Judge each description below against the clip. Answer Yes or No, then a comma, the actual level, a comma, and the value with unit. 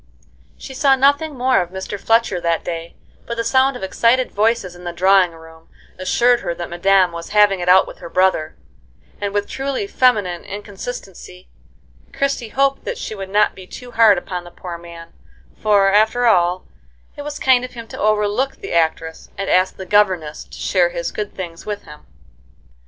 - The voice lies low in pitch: No, high, 195 Hz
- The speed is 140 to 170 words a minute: No, average, 185 wpm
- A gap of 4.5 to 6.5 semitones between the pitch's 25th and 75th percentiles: Yes, average, 5.1 semitones